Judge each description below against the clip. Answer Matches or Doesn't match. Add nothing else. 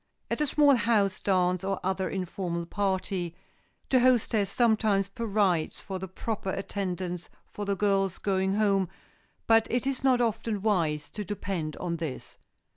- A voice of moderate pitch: Doesn't match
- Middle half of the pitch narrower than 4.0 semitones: Matches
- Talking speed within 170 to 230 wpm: Doesn't match